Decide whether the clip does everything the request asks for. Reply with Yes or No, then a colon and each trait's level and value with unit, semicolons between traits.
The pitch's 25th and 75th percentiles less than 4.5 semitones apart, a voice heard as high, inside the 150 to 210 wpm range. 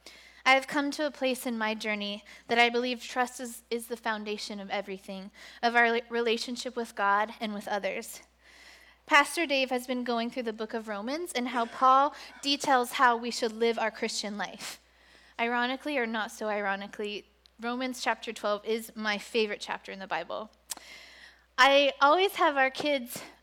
Yes: average, 3.2 semitones; high, 235 Hz; average, 175 wpm